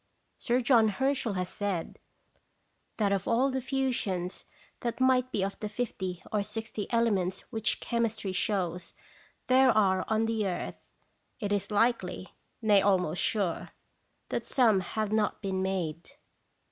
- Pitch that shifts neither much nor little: Yes, average, 3.6 semitones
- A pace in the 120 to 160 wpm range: Yes, average, 145 wpm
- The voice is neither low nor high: No, high, 210 Hz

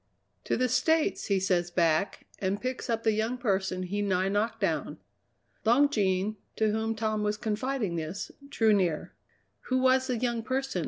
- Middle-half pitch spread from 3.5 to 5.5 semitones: Yes, average, 4.3 semitones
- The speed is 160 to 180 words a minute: Yes, average, 170 wpm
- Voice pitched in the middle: No, high, 215 Hz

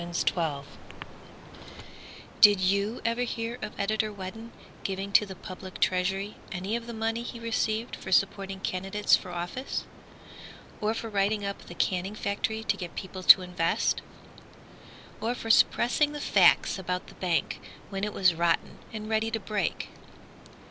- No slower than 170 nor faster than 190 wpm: No, average, 155 wpm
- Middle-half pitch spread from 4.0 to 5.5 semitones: No, average, 3.2 semitones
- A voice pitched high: Yes, high, 200 Hz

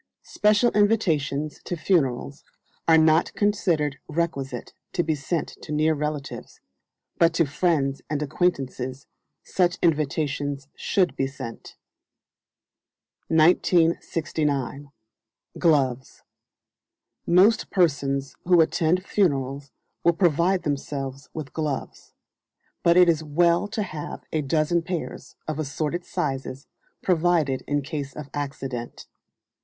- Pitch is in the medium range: Yes, medium, 155 Hz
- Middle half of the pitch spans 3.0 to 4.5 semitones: Yes, average, 3.7 semitones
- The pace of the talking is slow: Yes, slow, 105 wpm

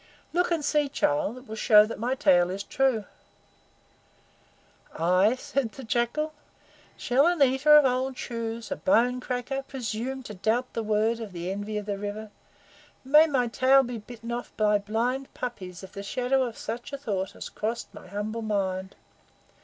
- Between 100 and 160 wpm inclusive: No, average, 175 wpm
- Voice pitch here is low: No, high, 235 Hz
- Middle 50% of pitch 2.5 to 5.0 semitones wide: Yes, average, 4.0 semitones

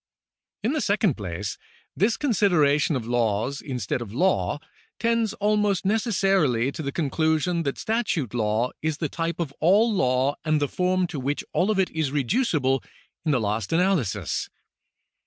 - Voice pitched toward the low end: No, medium, 155 Hz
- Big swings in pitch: Yes, wide, 7.1 semitones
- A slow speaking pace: No, average, 155 wpm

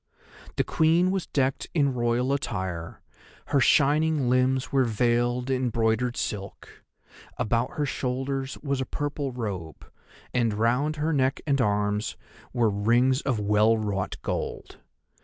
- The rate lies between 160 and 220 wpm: No, slow, 135 wpm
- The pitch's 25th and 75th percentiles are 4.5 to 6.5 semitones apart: No, average, 3.8 semitones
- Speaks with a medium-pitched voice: No, low, 125 Hz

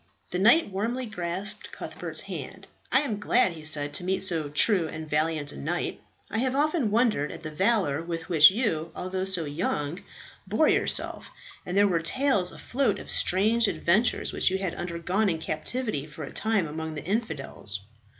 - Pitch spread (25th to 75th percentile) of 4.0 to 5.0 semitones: No, wide, 5.5 semitones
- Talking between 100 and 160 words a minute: No, average, 180 wpm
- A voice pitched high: No, medium, 180 Hz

